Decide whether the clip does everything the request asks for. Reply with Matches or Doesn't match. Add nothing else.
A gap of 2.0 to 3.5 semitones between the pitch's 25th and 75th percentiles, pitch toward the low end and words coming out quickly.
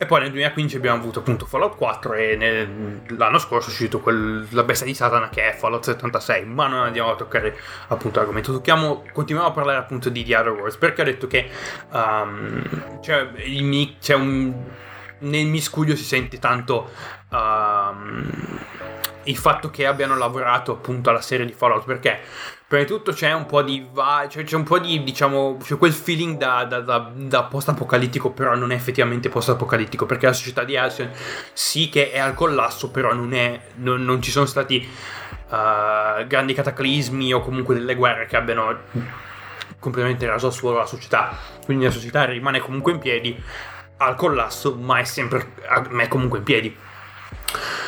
Matches